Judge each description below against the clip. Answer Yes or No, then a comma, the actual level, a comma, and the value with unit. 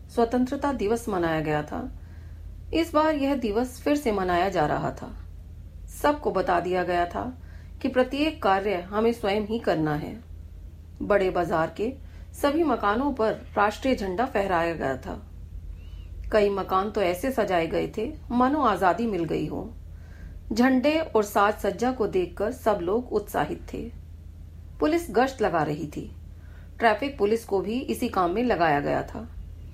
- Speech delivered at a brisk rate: No, average, 155 wpm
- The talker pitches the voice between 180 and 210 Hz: Yes, medium, 185 Hz